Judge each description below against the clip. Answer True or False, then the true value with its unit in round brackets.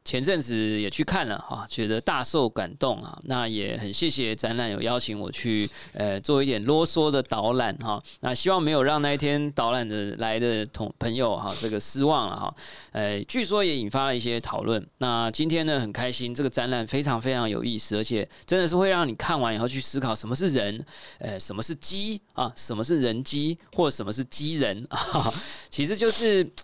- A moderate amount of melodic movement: False (5.7 semitones)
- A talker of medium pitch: False (125 Hz)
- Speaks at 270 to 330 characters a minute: True (295 characters per minute)